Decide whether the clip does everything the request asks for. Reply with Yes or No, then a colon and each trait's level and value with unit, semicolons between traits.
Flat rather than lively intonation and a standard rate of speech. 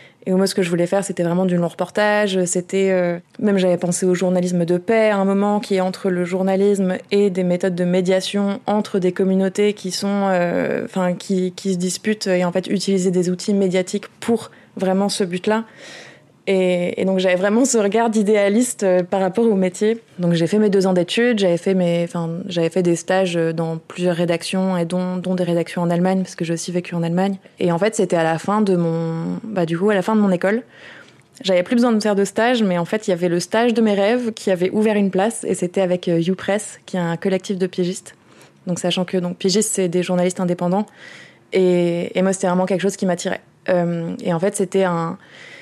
No: narrow, 2.1 semitones; fast, 230 wpm